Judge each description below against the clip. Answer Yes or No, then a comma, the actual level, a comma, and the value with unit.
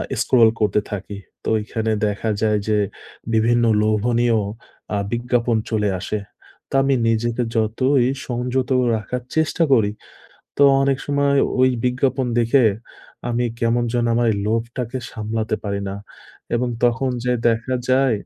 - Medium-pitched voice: No, low, 120 Hz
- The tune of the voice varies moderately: No, narrow, 2.3 semitones